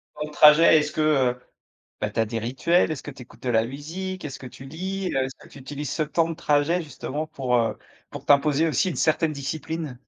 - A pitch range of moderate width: Yes, average, 3.4 semitones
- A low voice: No, medium, 150 Hz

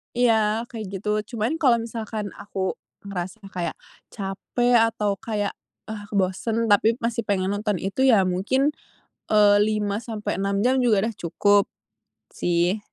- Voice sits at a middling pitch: No, high, 210 Hz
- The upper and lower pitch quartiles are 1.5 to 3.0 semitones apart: Yes, narrow, 2.5 semitones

